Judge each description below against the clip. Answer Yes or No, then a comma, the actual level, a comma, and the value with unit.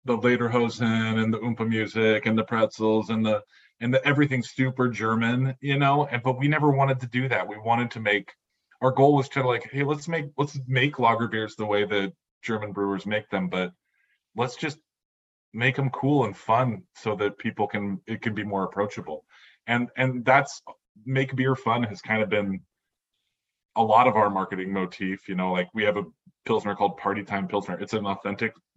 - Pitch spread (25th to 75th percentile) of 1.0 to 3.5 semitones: No, average, 4.2 semitones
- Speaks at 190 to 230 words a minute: Yes, average, 200 wpm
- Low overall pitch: Yes, low, 110 Hz